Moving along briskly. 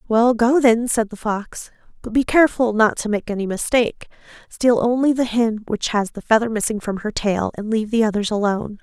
Yes: fast, 210 wpm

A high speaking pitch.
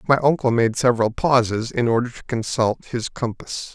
No: low, 120 Hz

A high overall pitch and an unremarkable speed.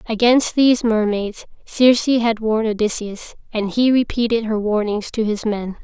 Yes: high, 225 Hz; average, 155 wpm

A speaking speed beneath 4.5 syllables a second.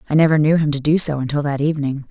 No: 7.4 syllables/s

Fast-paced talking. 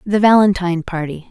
No: average, 140 wpm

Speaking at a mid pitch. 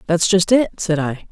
Yes: medium, 180 Hz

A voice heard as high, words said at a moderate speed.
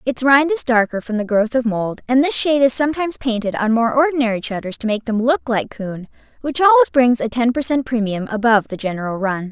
No: high, 240 Hz; fast, 225 wpm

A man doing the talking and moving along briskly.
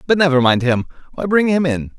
Yes: male; fast, 240 wpm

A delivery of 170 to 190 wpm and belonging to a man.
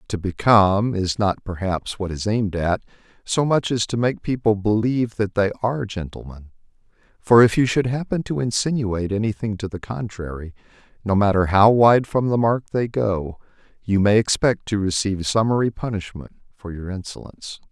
Yes: average, 175 wpm; male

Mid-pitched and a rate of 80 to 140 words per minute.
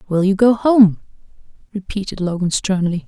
No: high, 200 Hz; slow, 135 wpm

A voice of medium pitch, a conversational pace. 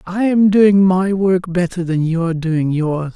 Yes: medium, 180 Hz; average, 190 wpm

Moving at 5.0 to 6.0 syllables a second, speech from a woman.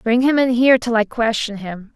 Yes: 5.2 syllables/s; female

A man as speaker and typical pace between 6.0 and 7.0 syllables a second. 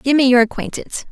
No: female; 6.7 syllables/s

